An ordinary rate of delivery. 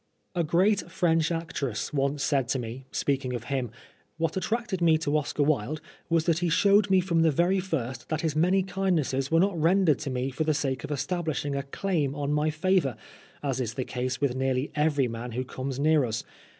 No: fast, 210 wpm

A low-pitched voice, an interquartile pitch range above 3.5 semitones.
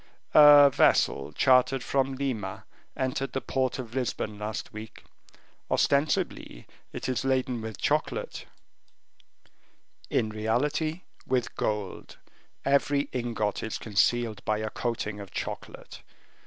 Yes: low, 125 Hz; average, 3.9 semitones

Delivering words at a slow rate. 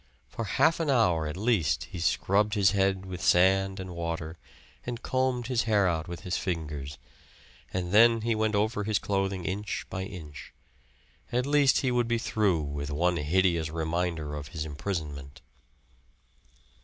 No: average, 160 wpm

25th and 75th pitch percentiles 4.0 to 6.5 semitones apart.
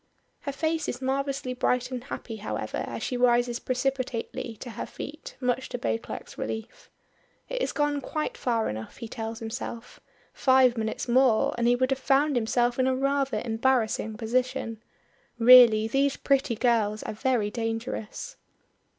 No: average, 3.0 semitones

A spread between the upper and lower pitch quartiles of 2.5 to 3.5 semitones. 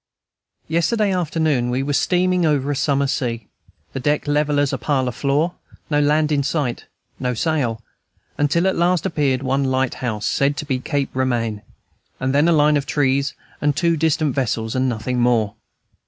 Yes: average, 2.9 semitones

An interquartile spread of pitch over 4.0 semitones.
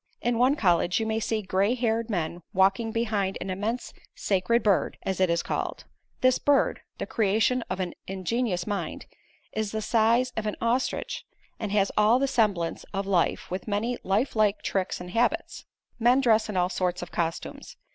No: average, 3.6 semitones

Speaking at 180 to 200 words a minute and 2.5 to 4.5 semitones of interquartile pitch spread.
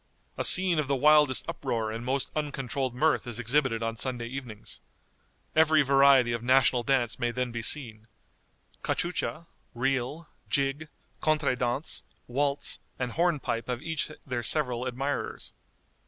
No: average, 140 wpm; average, 3.5 semitones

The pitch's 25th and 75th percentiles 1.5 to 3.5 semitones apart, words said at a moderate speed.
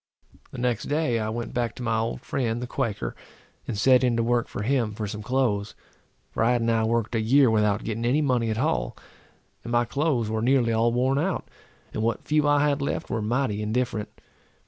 No: average, 2.8 semitones; fast, 215 wpm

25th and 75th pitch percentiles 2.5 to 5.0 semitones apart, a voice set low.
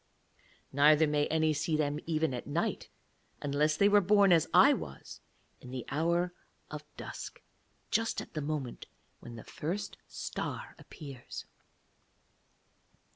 No: average, 3.0 semitones; medium, 155 Hz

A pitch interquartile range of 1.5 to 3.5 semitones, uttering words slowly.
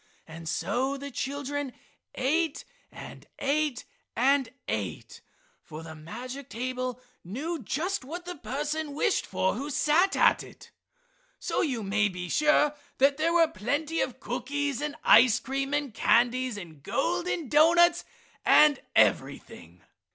No: average, 4.1 semitones; slow, 130 wpm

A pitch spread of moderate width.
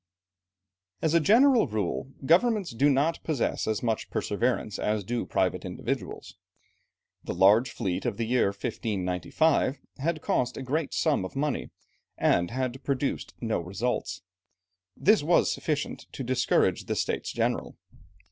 No: wide, 5.8 semitones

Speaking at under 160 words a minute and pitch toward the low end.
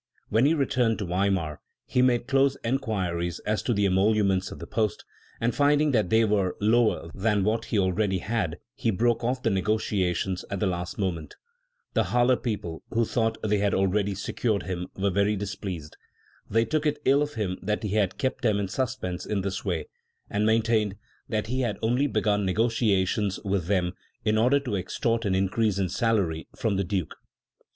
No: average, 190 wpm; low, 105 Hz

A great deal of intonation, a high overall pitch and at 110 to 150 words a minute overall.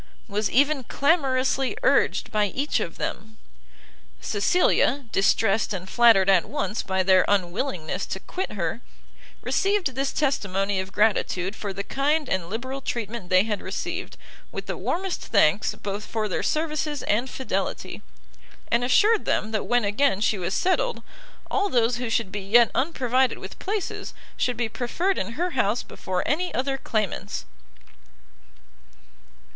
Yes: wide, 5.7 semitones; high, 230 Hz; average, 145 wpm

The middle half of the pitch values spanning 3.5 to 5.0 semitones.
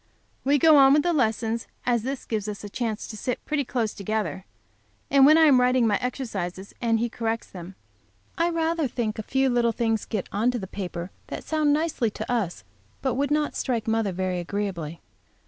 Yes: average, 4.5 semitones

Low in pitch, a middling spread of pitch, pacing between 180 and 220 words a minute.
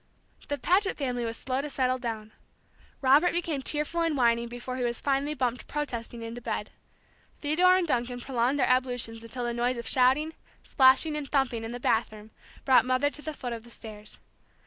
No: very high, 255 Hz; average, 3.5 semitones; average, 190 wpm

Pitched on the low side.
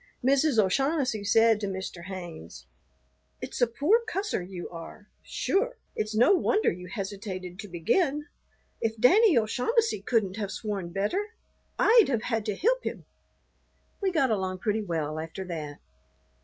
No: high, 215 Hz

